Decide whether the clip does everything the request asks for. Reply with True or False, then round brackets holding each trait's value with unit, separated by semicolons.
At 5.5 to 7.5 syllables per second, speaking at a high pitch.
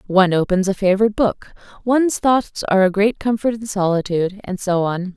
True (5.9 syllables/s; 200 Hz)